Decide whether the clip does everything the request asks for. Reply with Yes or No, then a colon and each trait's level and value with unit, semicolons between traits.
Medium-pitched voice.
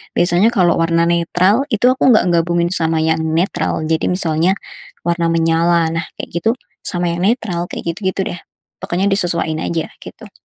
Yes: medium, 170 Hz